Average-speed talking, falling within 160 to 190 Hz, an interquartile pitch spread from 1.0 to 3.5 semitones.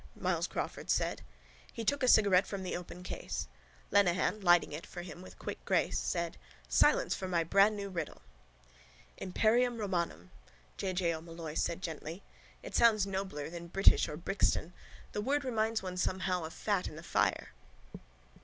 Yes: average, 160 wpm; medium, 185 Hz; average, 3.1 semitones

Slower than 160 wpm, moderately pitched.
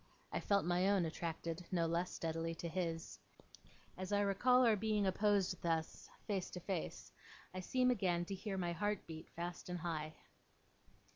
No: average, 165 wpm; medium, 180 Hz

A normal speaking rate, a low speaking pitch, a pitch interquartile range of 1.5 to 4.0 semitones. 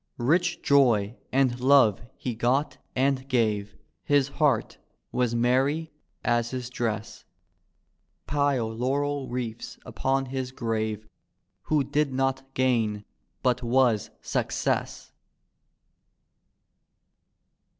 No: slow, 95 wpm; low, 125 Hz; average, 2.8 semitones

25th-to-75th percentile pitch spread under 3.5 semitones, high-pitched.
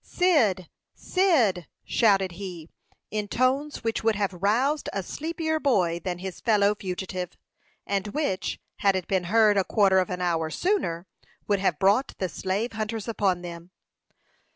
No: average, 3.9 semitones; high, 200 Hz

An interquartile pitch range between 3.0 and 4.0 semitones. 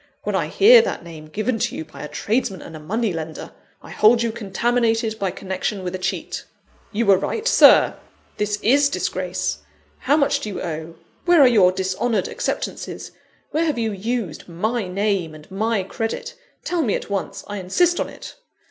No: average, 4.5 semitones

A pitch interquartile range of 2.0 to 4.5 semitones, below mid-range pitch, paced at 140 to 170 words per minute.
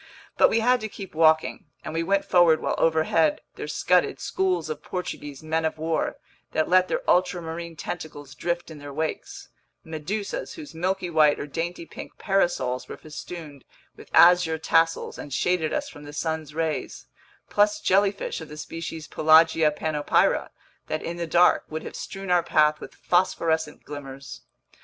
No: narrow, 2.4 semitones; medium, 160 Hz; average, 165 wpm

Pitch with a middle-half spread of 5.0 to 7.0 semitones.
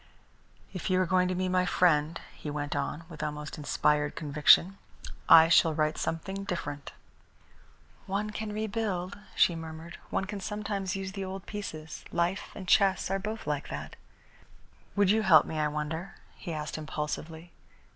No: average, 4.0 semitones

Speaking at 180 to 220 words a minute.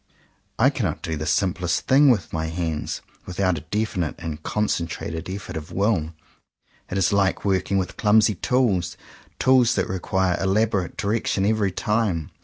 No: average, 160 wpm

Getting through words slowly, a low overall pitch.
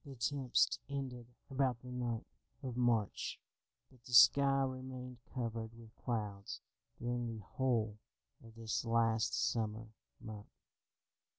Yes: slow, 120 wpm; low, 120 Hz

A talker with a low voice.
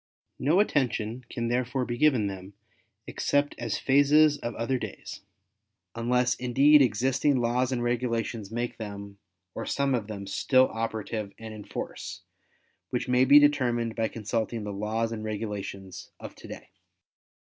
Yes: low, 120 Hz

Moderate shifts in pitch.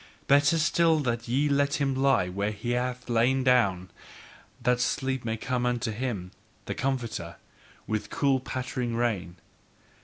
Yes: average, 3.1 semitones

